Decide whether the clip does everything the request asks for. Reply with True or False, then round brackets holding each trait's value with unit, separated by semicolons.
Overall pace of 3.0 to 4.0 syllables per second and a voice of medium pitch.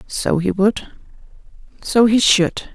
False (3.5 syllables/s; 205 Hz)